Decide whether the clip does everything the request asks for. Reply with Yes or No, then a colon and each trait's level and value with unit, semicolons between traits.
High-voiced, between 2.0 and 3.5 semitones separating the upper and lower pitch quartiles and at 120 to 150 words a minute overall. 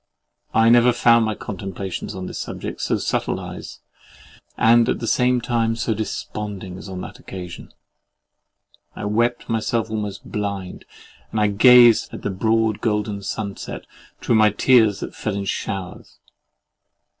No: low, 105 Hz; narrow, 2.6 semitones; average, 145 wpm